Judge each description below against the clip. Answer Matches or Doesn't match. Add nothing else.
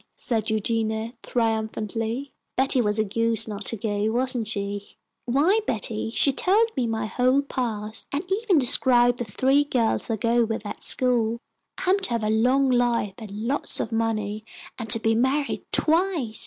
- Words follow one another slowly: Doesn't match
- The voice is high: Matches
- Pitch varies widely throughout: Doesn't match